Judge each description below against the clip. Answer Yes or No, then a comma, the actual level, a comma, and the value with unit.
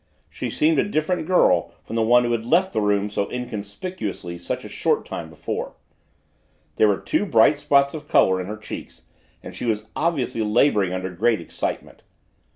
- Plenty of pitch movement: Yes, wide, 6.3 semitones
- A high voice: No, low, 115 Hz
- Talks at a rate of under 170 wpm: No, average, 180 wpm